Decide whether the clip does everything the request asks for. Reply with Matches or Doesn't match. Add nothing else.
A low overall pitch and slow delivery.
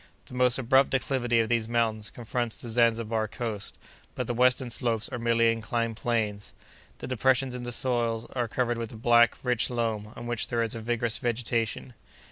Doesn't match